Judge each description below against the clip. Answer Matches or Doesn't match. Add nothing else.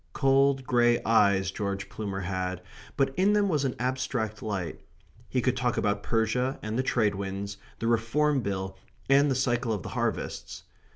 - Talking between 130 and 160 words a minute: Doesn't match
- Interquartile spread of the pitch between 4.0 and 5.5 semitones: Matches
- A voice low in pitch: Matches